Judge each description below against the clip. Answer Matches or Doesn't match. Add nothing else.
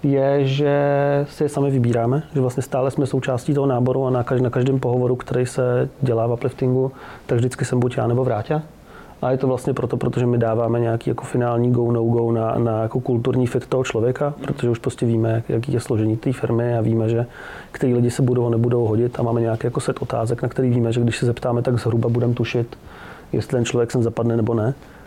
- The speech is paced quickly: Matches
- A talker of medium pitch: Doesn't match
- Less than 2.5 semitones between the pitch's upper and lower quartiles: Matches